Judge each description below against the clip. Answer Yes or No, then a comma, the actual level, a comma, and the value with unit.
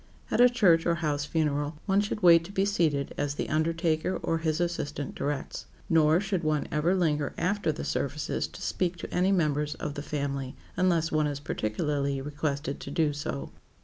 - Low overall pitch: No, medium, 155 Hz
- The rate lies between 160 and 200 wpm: Yes, average, 185 wpm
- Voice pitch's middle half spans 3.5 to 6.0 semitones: No, average, 3.0 semitones